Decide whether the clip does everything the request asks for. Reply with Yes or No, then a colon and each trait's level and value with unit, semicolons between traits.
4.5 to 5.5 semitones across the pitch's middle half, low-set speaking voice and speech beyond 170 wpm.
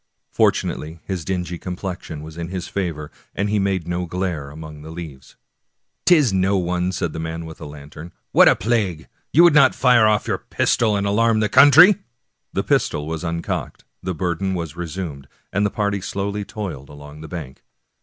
No: average, 4.1 semitones; very low, 90 Hz; average, 190 wpm